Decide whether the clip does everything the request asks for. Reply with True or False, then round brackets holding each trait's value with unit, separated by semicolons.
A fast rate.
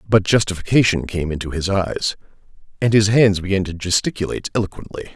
False (150 wpm)